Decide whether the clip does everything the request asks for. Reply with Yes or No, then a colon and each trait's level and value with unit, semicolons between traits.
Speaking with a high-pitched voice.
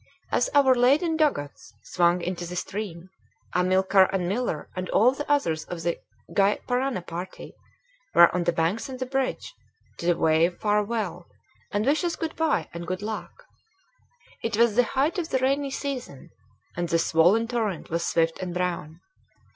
Yes: high, 195 Hz